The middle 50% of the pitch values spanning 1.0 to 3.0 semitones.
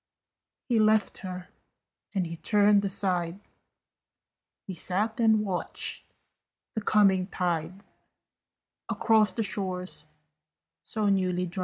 Yes: narrow, 2.6 semitones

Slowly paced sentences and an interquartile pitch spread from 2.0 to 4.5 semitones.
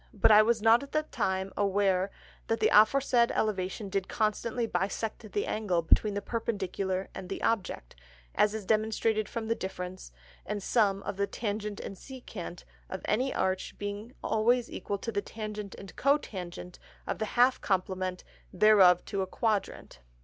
No: average, 165 wpm; average, 2.9 semitones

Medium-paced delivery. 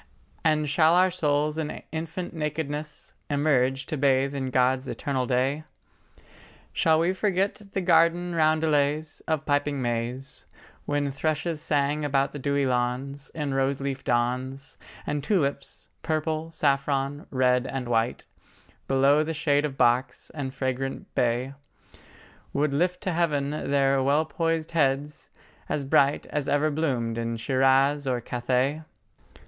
No: slow, 130 wpm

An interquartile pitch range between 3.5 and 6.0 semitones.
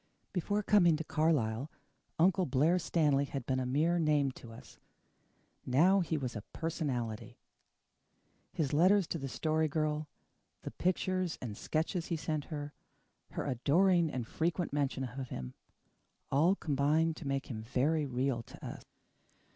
Yes: average, 4.1 semitones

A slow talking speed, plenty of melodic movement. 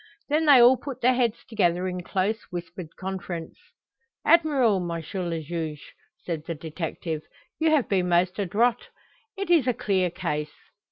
No: average, 155 wpm; wide, 6.4 semitones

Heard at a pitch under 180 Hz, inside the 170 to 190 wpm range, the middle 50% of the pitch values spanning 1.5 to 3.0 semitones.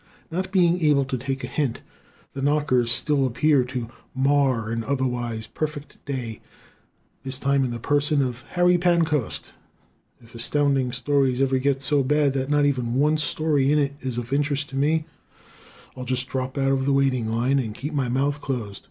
Yes: low, 135 Hz; average, 180 wpm; narrow, 2.5 semitones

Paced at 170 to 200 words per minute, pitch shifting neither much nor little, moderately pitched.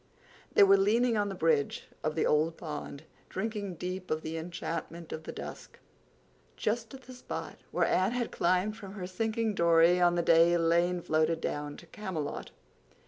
Yes: average, 175 wpm; average, 3.8 semitones; medium, 175 Hz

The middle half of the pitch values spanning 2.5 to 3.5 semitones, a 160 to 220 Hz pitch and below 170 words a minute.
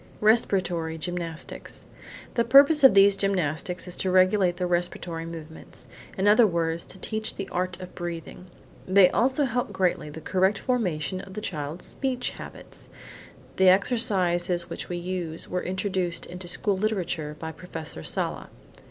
Yes: average, 2.9 semitones; medium, 185 Hz; average, 150 wpm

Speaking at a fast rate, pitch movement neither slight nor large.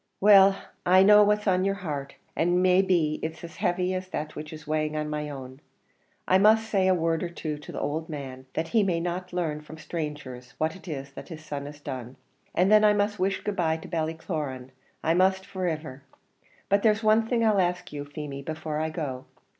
Yes: fast, 215 wpm; average, 4.0 semitones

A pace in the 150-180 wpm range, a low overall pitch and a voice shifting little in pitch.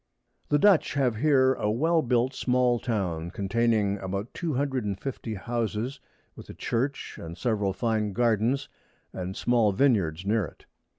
No: average, 160 wpm; low, 115 Hz; average, 4.5 semitones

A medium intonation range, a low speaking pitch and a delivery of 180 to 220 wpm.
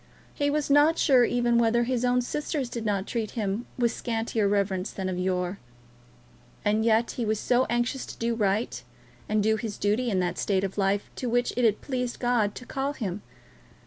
No: average, 3.3 semitones; high, 230 Hz; average, 200 wpm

